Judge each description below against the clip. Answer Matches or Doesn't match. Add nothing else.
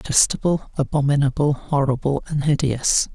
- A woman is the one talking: Doesn't match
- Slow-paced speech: Matches